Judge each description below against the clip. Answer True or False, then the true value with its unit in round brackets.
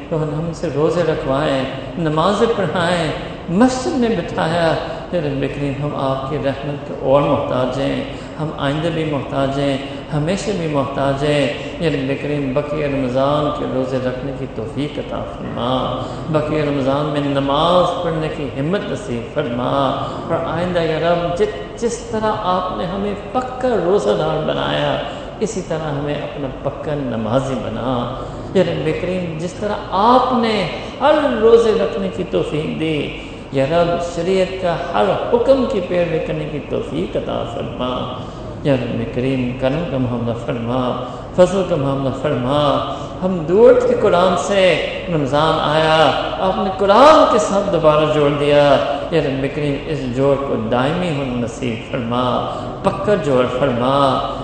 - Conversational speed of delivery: True (145 wpm)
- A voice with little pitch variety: False (4.6 semitones)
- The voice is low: False (150 Hz)